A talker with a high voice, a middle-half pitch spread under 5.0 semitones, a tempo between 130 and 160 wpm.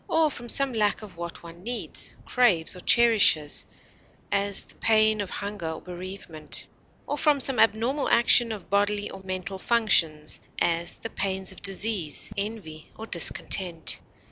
Yes: high, 200 Hz; average, 4.4 semitones; average, 150 wpm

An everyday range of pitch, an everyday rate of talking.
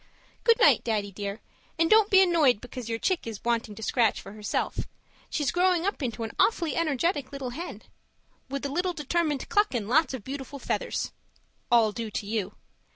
No: wide, 6.8 semitones; average, 185 wpm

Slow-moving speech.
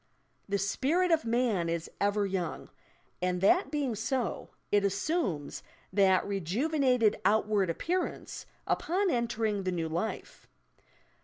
Yes: slow, 115 wpm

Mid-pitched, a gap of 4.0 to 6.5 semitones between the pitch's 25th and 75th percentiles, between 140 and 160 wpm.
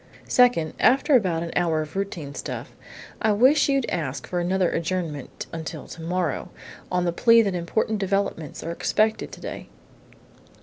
Yes: medium, 180 Hz; average, 4.7 semitones; average, 145 wpm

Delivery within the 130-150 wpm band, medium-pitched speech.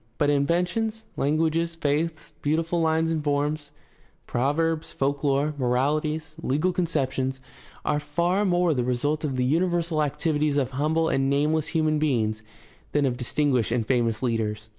Yes: average, 140 wpm; medium, 150 Hz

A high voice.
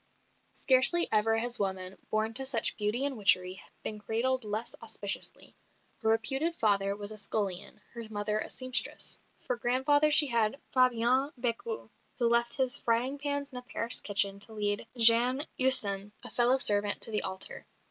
Yes: high, 230 Hz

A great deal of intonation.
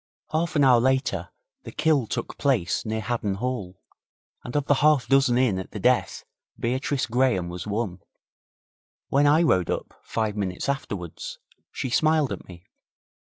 Yes: wide, 5.8 semitones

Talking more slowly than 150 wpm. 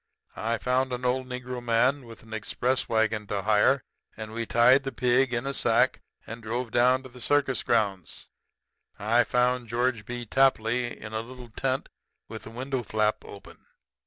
No: average, 175 wpm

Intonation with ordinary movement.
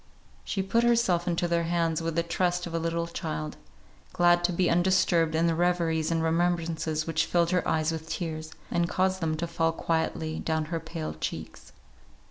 No: narrow, 1.4 semitones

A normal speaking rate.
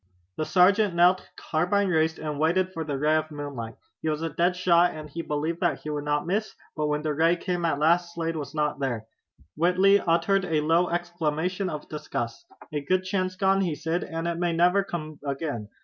No: fast, 210 wpm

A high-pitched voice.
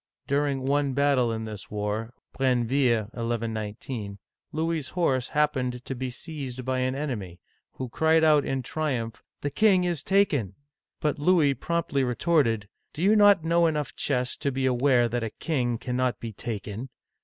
No: low, 130 Hz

